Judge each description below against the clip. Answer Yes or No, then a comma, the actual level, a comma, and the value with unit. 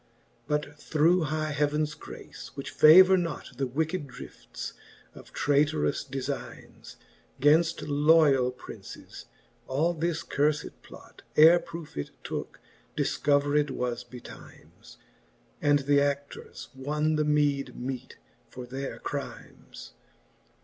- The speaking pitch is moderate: Yes, medium, 145 Hz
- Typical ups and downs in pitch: No, narrow, 2.1 semitones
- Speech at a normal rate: No, slow, 110 wpm